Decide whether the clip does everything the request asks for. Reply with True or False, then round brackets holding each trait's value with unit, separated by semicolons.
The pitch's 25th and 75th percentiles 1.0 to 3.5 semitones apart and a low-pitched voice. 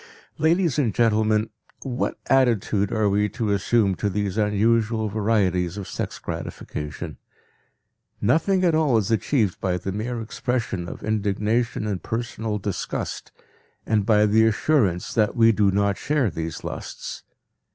True (2.7 semitones; 110 Hz)